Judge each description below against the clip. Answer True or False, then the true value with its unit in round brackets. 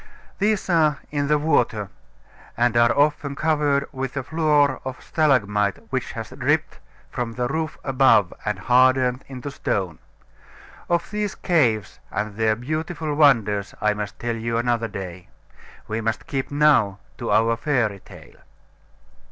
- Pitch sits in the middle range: False (125 Hz)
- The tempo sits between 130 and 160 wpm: True (145 wpm)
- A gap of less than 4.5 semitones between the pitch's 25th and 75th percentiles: False (5.3 semitones)